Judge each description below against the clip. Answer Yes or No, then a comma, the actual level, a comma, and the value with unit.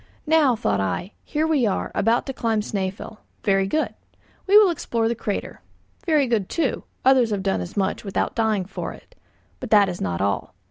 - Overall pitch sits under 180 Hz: No, high, 220 Hz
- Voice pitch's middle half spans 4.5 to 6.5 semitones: Yes, wide, 5.5 semitones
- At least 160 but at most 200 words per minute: Yes, average, 190 wpm